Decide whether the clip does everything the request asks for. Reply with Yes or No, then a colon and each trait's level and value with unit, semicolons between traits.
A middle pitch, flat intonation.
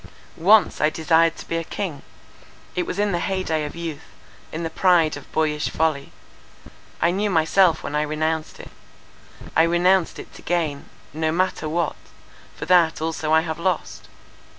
Yes: medium, 165 Hz; narrow, 2.0 semitones